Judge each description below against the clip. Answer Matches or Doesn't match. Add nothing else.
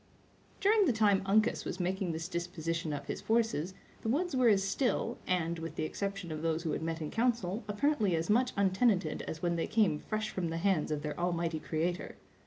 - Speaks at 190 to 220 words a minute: Matches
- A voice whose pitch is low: Doesn't match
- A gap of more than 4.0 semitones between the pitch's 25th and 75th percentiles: Matches